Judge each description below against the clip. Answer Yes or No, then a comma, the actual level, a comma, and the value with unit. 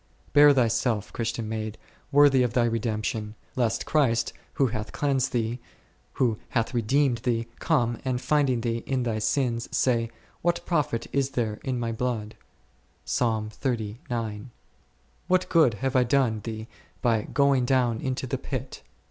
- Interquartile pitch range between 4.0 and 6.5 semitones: No, average, 3.0 semitones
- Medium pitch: No, low, 120 Hz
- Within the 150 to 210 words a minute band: No, average, 140 wpm